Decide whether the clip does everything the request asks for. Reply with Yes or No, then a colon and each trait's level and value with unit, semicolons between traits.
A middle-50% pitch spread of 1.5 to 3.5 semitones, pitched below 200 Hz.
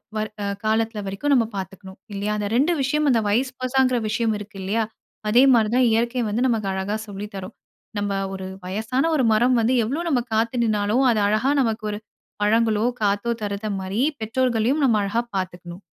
No: average, 3.2 semitones; high, 220 Hz